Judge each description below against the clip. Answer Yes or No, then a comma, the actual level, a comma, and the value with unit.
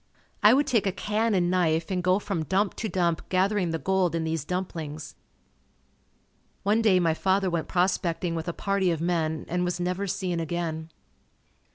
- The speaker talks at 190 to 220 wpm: No, average, 180 wpm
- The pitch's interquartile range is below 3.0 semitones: Yes, narrow, 2.6 semitones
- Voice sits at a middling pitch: Yes, medium, 180 Hz